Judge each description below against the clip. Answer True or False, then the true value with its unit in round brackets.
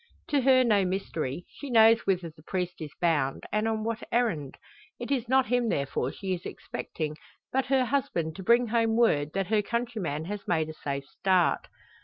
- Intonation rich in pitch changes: True (6.7 semitones)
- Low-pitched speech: False (200 Hz)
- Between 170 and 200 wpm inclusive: True (190 wpm)